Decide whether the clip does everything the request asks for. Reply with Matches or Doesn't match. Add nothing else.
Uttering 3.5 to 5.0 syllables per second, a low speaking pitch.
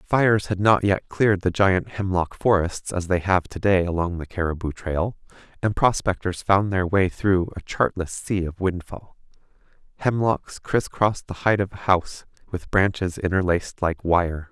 Matches